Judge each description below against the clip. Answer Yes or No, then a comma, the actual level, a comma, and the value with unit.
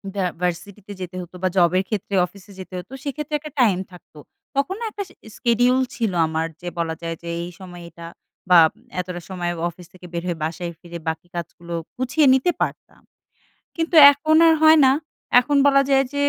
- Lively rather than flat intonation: Yes, wide, 7.5 semitones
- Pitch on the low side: No, medium, 185 Hz